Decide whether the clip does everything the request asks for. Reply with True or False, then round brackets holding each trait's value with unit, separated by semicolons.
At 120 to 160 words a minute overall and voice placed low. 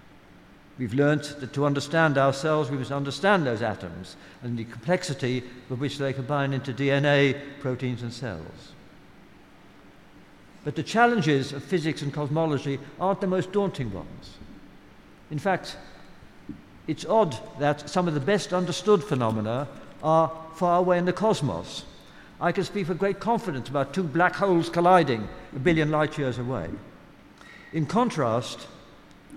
False (145 wpm; 145 Hz)